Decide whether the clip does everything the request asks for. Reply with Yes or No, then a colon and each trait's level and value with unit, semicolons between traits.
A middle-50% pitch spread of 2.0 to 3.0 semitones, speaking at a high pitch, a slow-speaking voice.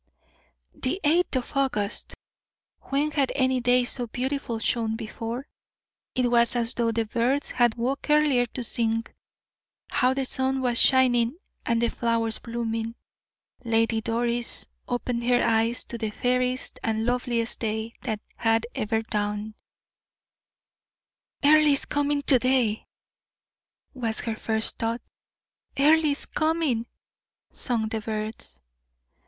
Yes: narrow, 2.5 semitones; high, 240 Hz; slow, 125 wpm